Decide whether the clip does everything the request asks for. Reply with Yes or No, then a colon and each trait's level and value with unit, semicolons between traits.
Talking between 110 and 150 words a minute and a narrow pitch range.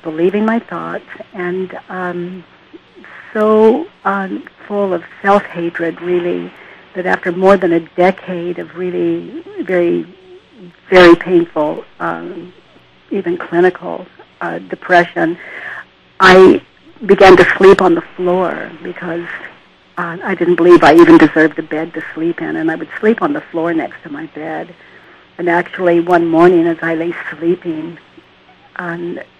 Yes: average, 140 wpm; narrow, 2.3 semitones